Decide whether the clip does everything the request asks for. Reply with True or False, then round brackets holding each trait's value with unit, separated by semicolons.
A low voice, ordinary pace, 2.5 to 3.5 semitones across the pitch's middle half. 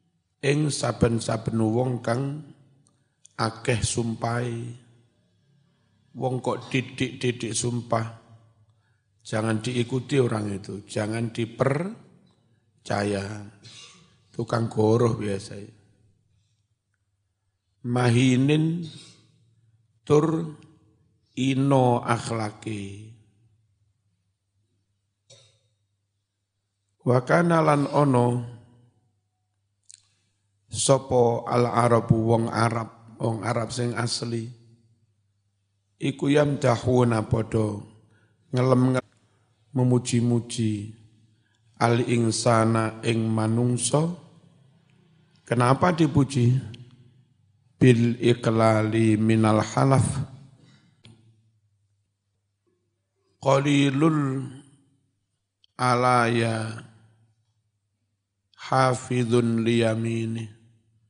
False (115 Hz; 55 wpm; 2.8 semitones)